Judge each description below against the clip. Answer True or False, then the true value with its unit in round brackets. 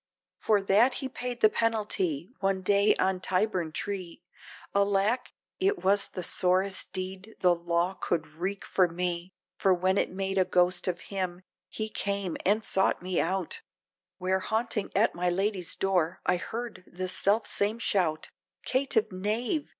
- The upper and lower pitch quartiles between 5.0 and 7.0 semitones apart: False (2.6 semitones)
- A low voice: False (190 Hz)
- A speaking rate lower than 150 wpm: False (160 wpm)